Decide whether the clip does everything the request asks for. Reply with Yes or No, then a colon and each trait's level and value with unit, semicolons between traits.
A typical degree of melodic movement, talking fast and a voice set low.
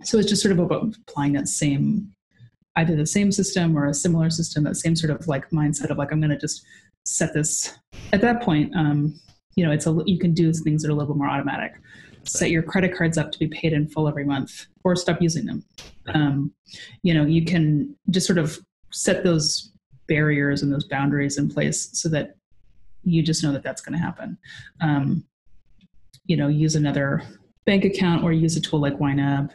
No: average, 3.1 semitones; fast, 215 wpm; medium, 155 Hz